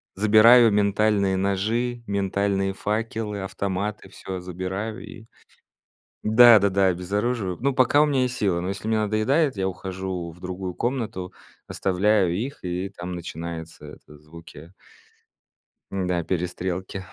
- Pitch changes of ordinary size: Yes, average, 3.0 semitones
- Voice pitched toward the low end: Yes, low, 100 Hz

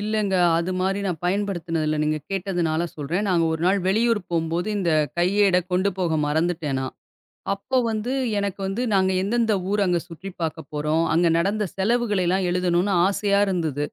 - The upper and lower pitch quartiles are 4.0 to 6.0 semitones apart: No, average, 3.3 semitones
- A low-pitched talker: No, medium, 185 Hz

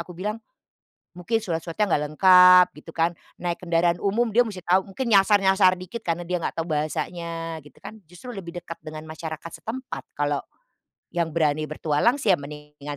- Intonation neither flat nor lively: Yes, average, 3.4 semitones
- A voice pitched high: No, medium, 175 Hz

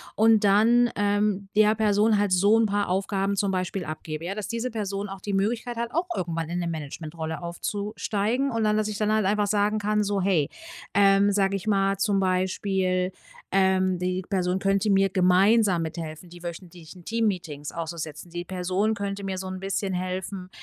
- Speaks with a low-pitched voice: No, high, 195 Hz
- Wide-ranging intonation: No, narrow, 2.5 semitones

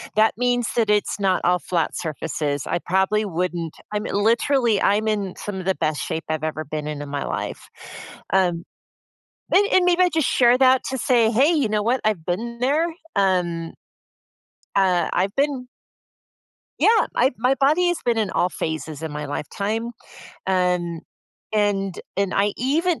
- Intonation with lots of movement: Yes, wide, 6.0 semitones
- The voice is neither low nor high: No, high, 205 Hz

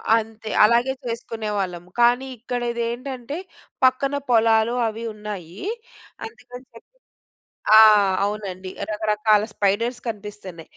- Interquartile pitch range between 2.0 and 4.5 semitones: Yes, narrow, 2.6 semitones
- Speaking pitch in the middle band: No, high, 225 Hz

